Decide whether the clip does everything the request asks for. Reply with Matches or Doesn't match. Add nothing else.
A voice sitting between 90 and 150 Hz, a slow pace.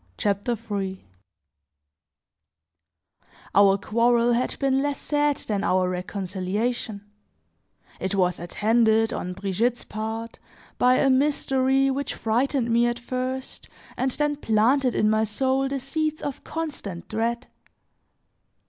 Doesn't match